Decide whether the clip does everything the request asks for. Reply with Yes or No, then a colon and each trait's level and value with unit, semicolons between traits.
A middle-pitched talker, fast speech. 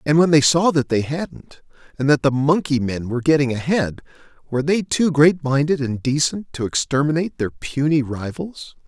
No: medium, 145 Hz; average, 185 wpm